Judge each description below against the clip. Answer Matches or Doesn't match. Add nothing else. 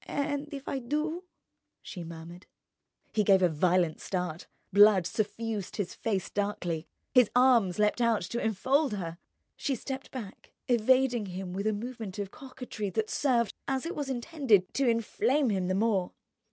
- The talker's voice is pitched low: Doesn't match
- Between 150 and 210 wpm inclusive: Matches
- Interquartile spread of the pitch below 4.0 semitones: Doesn't match